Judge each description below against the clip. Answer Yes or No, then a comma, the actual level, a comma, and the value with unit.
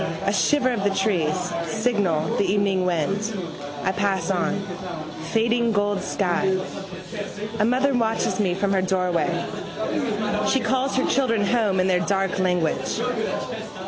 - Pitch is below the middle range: No, high, 200 Hz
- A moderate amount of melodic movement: Yes, average, 3.5 semitones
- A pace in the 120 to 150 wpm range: Yes, slow, 135 wpm